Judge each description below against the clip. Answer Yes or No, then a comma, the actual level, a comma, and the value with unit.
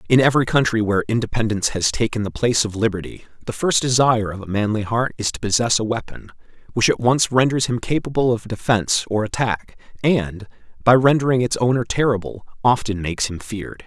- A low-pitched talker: Yes, low, 115 Hz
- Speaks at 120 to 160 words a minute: No, average, 185 wpm